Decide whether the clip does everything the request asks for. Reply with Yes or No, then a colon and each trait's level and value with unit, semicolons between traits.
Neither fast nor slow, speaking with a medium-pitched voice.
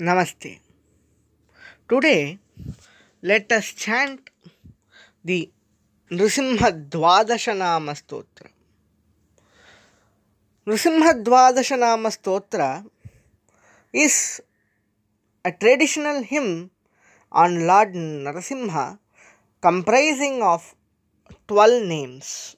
No: slow, 55 wpm; medium, 180 Hz